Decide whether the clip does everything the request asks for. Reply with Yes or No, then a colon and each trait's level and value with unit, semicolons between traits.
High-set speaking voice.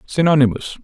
No: medium, 140 Hz